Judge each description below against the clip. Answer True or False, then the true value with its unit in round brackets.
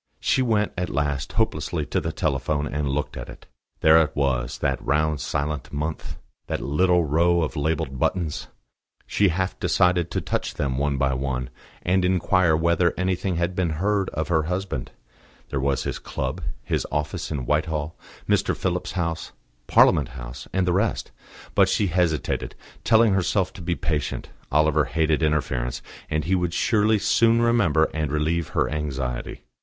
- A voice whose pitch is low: True (80 Hz)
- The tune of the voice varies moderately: True (3.8 semitones)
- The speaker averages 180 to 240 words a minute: False (165 wpm)